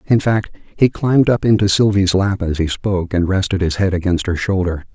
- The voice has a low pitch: Yes, very low, 95 Hz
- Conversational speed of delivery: No, fast, 220 wpm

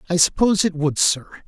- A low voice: No, medium, 170 Hz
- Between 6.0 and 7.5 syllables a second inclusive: Yes, 6.1 syllables/s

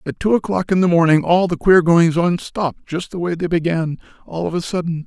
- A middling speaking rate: No, fast, 235 wpm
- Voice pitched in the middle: Yes, medium, 170 Hz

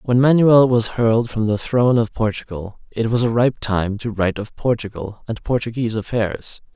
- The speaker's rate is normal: Yes, average, 185 wpm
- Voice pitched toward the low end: Yes, low, 115 Hz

